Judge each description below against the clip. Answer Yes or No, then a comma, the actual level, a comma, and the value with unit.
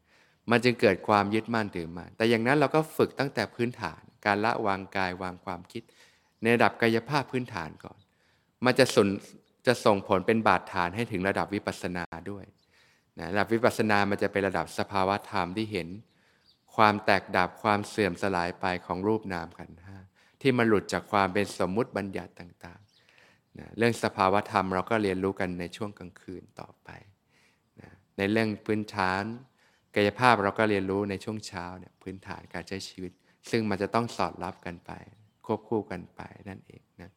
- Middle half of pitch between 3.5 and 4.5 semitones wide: No, average, 3.1 semitones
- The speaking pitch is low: Yes, low, 100 Hz